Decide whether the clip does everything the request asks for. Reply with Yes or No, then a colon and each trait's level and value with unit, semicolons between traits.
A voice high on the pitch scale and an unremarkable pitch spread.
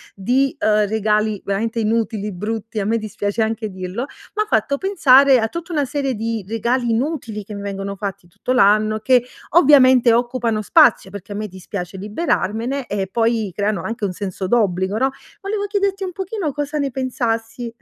Yes: high, 225 Hz; average, 4.3 semitones